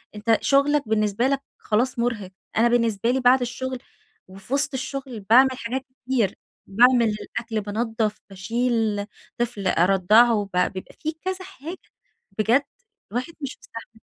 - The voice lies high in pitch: Yes, high, 235 Hz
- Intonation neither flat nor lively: Yes, average, 3.7 semitones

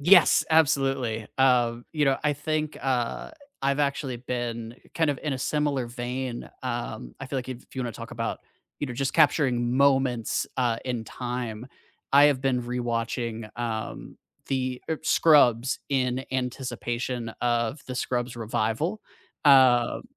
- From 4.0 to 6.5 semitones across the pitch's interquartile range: No, narrow, 2.5 semitones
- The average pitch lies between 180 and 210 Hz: No, low, 125 Hz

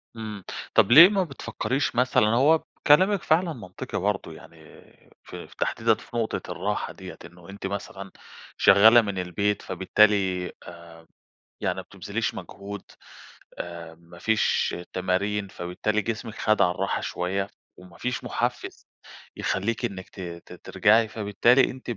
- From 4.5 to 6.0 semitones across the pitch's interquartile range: No, average, 4.1 semitones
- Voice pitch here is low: Yes, low, 100 Hz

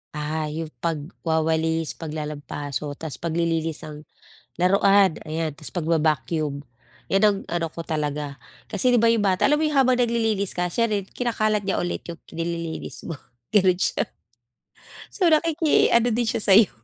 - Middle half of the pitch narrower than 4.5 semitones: No, average, 5.3 semitones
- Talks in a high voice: No, medium, 170 Hz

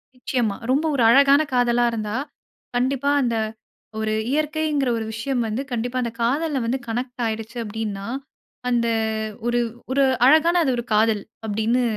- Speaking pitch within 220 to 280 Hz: Yes, high, 245 Hz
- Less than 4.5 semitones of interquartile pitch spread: Yes, average, 3.6 semitones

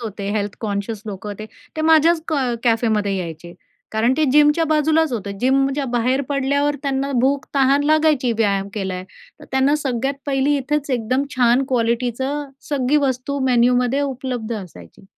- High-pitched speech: Yes, very high, 255 Hz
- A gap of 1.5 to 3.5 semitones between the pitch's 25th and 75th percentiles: No, average, 4.3 semitones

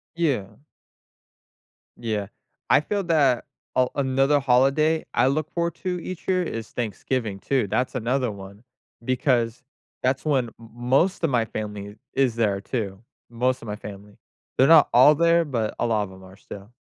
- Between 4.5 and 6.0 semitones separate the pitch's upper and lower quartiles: Yes, average, 5.1 semitones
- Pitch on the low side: Yes, low, 125 Hz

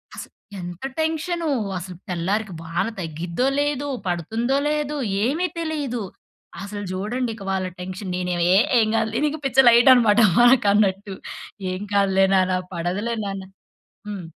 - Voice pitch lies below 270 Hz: Yes, high, 205 Hz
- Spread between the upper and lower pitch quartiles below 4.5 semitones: No, wide, 5.6 semitones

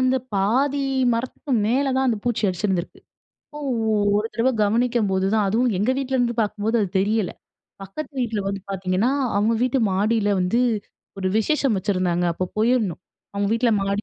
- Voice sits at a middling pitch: No, high, 215 Hz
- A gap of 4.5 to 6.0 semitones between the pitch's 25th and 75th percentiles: No, average, 3.9 semitones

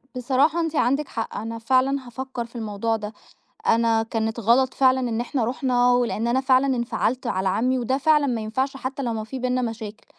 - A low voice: No, high, 245 Hz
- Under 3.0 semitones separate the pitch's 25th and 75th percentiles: Yes, narrow, 2.5 semitones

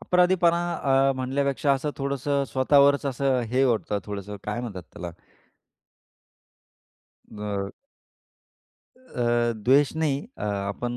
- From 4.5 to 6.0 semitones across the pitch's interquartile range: Yes, average, 5.0 semitones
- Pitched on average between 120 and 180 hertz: Yes, low, 135 Hz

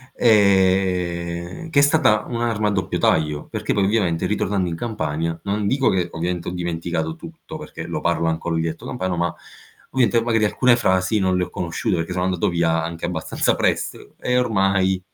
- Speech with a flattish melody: No, average, 4.0 semitones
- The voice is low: Yes, very low, 95 Hz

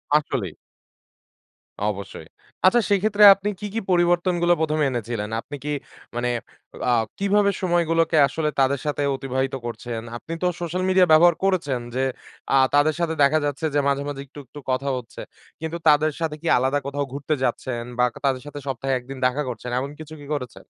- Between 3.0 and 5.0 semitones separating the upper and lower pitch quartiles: Yes, average, 4.5 semitones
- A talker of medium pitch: Yes, medium, 145 Hz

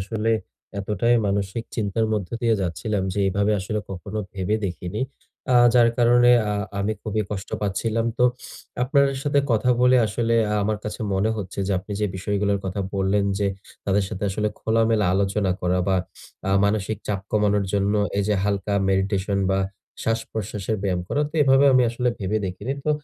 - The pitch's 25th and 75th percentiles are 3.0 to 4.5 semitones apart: No, narrow, 2.5 semitones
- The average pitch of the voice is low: Yes, low, 105 Hz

